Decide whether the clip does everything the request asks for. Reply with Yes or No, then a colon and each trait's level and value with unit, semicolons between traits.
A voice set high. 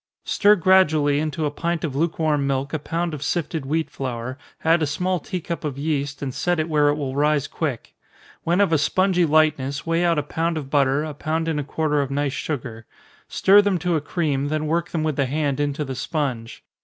No: medium, 150 Hz